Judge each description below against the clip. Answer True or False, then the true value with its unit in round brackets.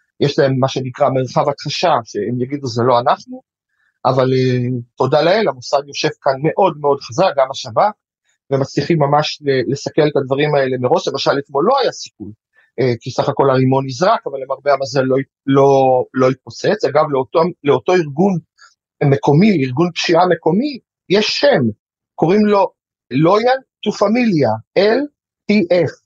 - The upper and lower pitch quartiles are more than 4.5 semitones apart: True (4.9 semitones)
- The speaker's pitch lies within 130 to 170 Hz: True (140 Hz)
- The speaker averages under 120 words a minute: False (145 wpm)